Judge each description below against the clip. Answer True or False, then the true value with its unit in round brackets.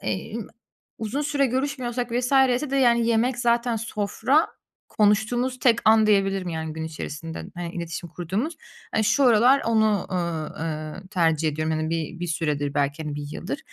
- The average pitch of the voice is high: True (205 Hz)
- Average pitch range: False (7.0 semitones)